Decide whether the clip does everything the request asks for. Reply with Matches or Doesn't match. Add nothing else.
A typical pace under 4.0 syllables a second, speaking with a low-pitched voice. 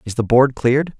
Doesn't match